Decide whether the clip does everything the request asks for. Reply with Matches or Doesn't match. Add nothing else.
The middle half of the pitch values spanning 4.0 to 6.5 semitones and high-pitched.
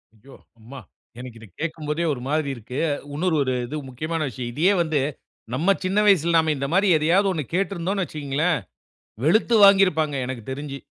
Doesn't match